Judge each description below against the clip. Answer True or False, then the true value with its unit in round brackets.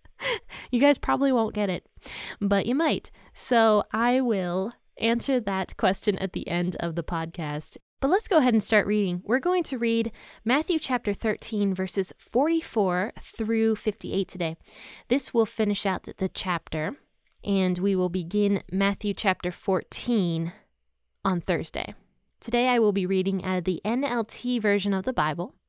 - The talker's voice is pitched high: True (205 Hz)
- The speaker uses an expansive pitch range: False (4.2 semitones)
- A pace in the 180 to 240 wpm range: False (160 wpm)